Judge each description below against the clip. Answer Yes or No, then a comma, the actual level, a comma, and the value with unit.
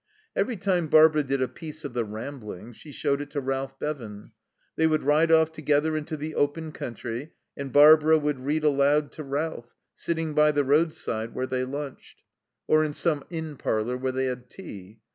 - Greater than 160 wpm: Yes, average, 185 wpm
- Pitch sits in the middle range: Yes, medium, 145 Hz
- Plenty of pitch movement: No, average, 3.2 semitones